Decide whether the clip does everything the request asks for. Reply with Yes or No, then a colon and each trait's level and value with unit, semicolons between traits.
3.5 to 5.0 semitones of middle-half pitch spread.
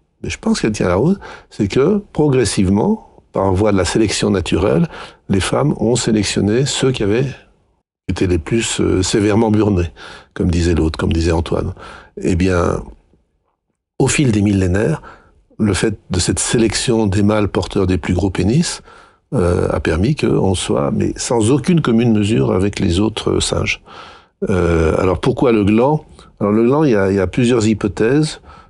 Yes: average, 4.2 semitones